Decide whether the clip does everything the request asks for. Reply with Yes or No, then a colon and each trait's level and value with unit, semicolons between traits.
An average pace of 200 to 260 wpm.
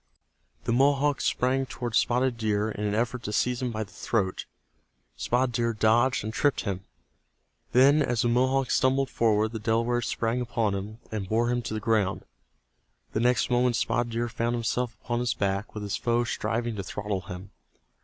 No: average, 185 wpm